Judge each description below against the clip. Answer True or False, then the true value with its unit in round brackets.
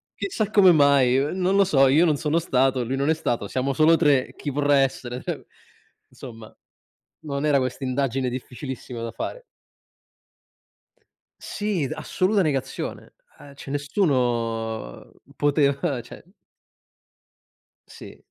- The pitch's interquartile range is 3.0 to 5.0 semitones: True (3.4 semitones)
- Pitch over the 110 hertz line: True (140 Hz)